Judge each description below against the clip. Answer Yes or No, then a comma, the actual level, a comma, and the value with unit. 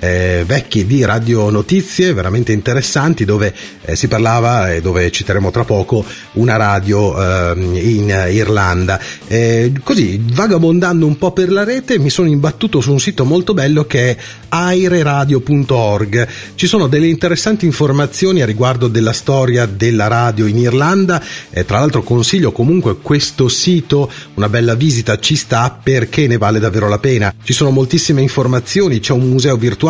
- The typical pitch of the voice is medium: No, low, 125 Hz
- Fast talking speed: No, average, 160 wpm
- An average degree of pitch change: No, wide, 5.7 semitones